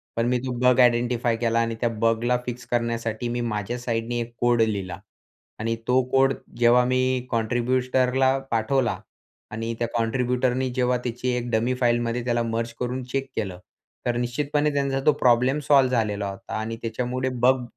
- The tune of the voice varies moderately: No, narrow, 1.7 semitones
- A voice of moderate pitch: No, low, 120 Hz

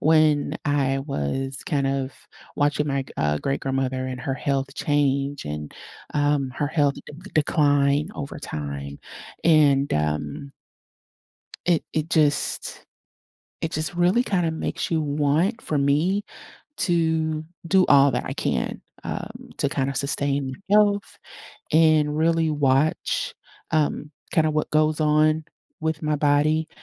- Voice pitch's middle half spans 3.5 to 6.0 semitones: No, narrow, 2.4 semitones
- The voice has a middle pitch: Yes, medium, 145 Hz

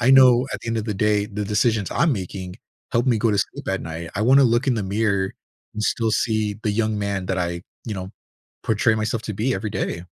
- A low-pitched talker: Yes, low, 105 Hz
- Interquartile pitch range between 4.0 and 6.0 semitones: No, average, 2.7 semitones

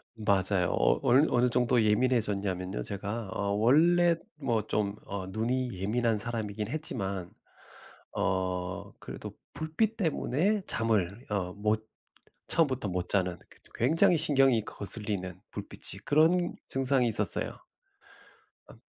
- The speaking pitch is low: Yes, low, 110 Hz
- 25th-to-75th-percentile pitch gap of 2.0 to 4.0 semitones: No, average, 5.1 semitones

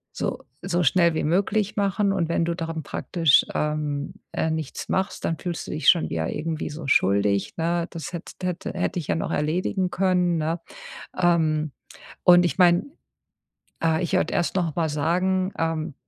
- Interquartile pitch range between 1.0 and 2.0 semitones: No, narrow, 2.5 semitones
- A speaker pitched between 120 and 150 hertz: No, medium, 170 Hz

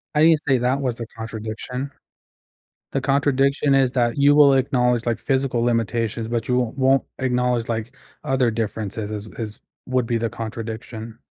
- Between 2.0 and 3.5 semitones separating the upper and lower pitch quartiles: Yes, average, 2.8 semitones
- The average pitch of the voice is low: Yes, low, 125 Hz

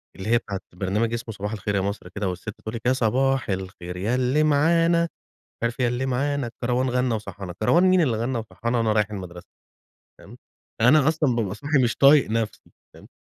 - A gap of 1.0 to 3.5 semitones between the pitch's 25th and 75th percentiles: No, average, 4.4 semitones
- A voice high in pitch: No, low, 115 Hz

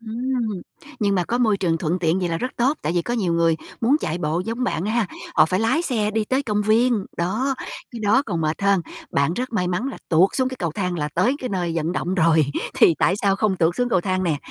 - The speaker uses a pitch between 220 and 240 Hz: No, high, 195 Hz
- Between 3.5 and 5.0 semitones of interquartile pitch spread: No, wide, 5.4 semitones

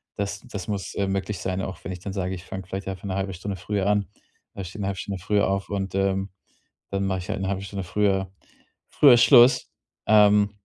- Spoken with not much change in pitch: Yes, narrow, 1.2 semitones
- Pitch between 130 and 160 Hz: No, very low, 95 Hz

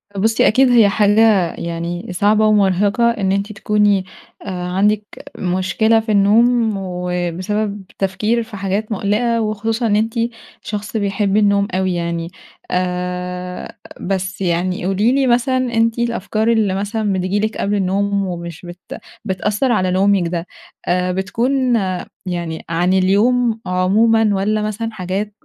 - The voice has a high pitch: Yes, high, 200 Hz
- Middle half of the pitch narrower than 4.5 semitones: Yes, average, 3.1 semitones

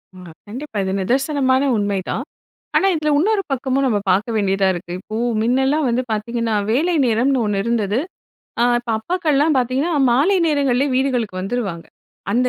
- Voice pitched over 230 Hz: Yes, very high, 250 Hz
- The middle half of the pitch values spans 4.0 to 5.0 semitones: Yes, average, 4.6 semitones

